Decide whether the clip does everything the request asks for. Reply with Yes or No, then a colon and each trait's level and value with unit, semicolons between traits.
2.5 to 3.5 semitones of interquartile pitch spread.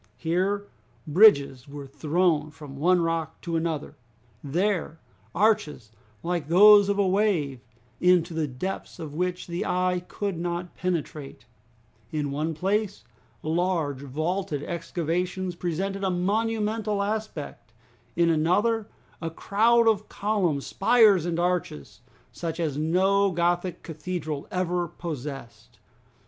No: average, 3.9 semitones